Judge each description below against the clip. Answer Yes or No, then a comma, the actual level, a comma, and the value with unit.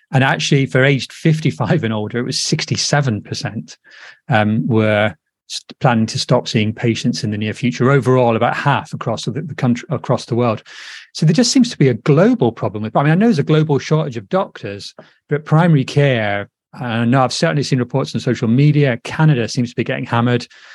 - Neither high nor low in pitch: No, low, 130 Hz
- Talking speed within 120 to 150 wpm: No, fast, 205 wpm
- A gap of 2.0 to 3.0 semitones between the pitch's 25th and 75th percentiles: No, average, 3.6 semitones